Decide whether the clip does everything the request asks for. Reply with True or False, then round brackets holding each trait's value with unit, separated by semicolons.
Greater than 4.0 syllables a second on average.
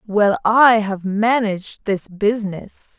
False (3.8 syllables/s)